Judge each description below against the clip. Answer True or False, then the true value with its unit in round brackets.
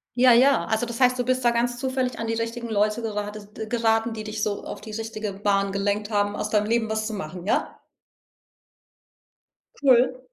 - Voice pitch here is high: True (225 Hz)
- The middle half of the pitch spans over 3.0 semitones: False (2.4 semitones)